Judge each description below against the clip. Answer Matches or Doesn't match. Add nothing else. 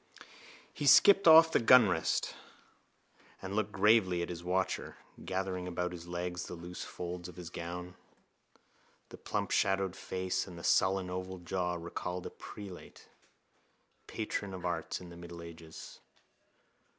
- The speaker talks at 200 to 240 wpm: Doesn't match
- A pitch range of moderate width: Doesn't match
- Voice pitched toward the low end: Matches